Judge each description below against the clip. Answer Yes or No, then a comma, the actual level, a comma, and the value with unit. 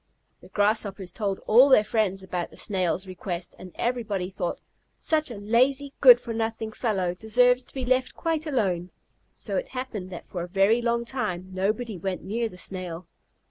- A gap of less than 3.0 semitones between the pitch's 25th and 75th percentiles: No, average, 4.8 semitones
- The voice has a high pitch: Yes, high, 215 Hz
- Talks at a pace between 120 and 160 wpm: No, average, 180 wpm